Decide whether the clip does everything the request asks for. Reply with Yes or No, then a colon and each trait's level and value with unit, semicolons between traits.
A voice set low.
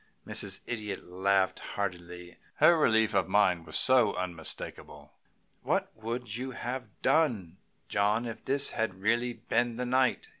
Yes: low, 110 Hz